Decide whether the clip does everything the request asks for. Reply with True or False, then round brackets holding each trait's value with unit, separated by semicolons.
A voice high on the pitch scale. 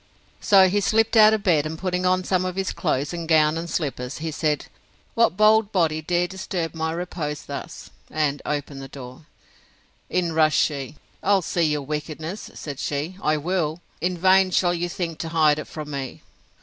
False (165 Hz)